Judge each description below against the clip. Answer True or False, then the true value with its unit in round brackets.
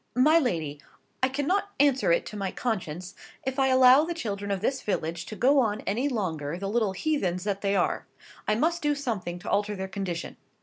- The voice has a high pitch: True (210 Hz)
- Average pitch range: False (6.2 semitones)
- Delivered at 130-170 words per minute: False (205 wpm)